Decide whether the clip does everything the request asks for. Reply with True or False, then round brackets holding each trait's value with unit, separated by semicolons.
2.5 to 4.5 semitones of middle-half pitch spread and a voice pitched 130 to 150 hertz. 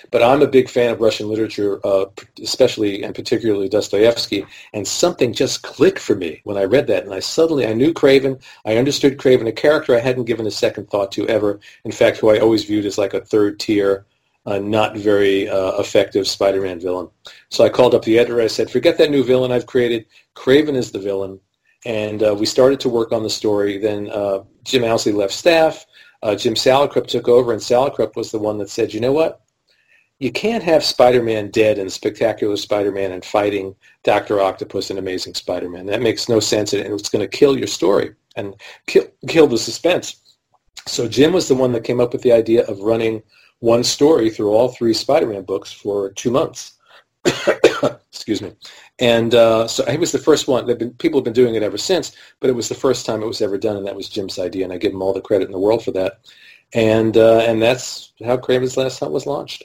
False (3.7 semitones; 115 Hz)